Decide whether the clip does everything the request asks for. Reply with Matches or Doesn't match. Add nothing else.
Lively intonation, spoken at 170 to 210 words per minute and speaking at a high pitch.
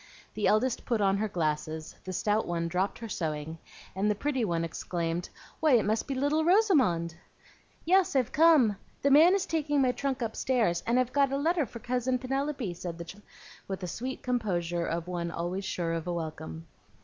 Matches